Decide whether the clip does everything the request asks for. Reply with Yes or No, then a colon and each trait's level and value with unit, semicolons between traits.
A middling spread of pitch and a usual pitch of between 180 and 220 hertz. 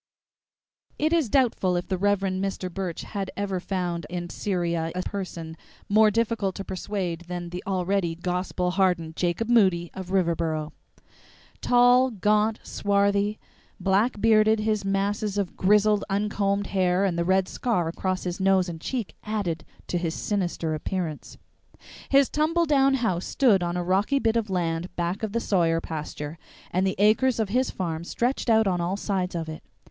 Yes: average, 3.3 semitones; high, 190 Hz